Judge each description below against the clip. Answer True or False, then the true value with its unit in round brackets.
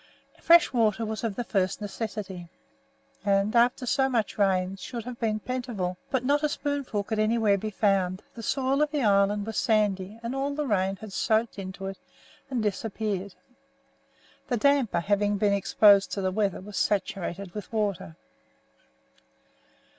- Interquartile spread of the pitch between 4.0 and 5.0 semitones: False (3.3 semitones)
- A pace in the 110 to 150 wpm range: False (160 wpm)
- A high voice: True (210 Hz)